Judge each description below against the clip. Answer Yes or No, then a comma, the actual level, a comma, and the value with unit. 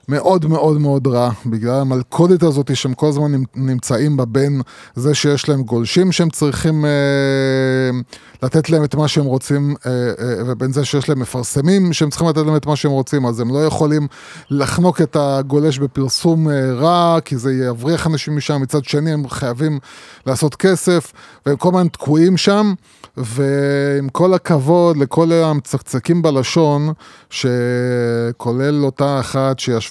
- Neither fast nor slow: No, fast, 155 wpm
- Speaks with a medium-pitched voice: Yes, medium, 145 Hz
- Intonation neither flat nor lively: Yes, average, 3.1 semitones